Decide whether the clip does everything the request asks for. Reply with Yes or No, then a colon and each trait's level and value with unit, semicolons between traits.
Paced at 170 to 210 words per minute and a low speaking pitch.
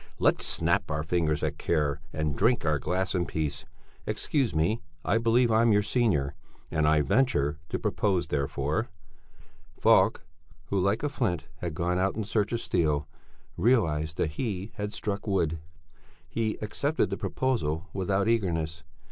No: average, 155 wpm; very low, 90 Hz